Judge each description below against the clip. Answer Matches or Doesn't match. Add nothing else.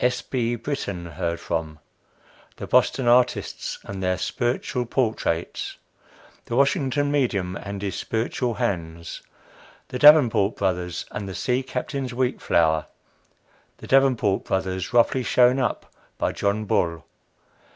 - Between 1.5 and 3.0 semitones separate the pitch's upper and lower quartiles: Doesn't match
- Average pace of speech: Doesn't match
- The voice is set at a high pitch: Doesn't match